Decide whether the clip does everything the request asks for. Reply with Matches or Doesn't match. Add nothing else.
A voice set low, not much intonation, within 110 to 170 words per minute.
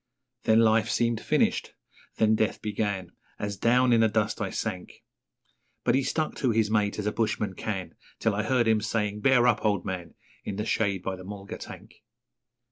Doesn't match